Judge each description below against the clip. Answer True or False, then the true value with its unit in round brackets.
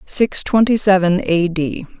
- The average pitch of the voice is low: False (190 Hz)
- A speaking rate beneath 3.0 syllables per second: True (1.7 syllables/s)